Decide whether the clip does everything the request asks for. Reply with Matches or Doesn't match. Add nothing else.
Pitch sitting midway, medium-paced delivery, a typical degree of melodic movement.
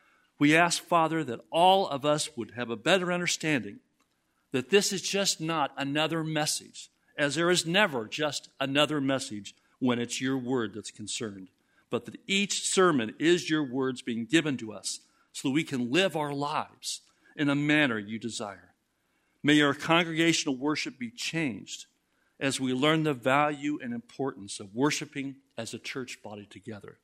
Matches